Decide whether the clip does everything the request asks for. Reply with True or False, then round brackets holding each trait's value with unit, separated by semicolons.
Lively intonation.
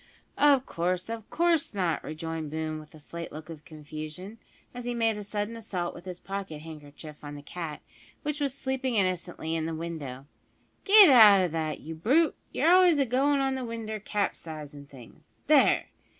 True (7.4 semitones)